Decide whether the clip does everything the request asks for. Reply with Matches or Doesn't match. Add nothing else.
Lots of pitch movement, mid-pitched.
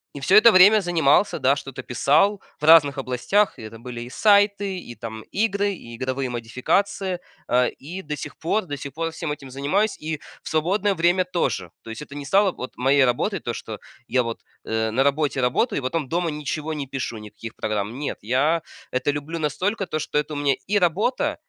Matches